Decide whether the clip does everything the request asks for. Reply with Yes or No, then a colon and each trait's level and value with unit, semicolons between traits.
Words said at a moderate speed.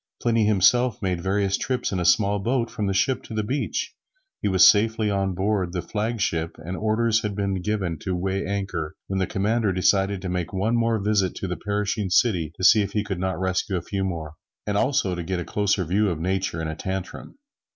No: fast, 225 wpm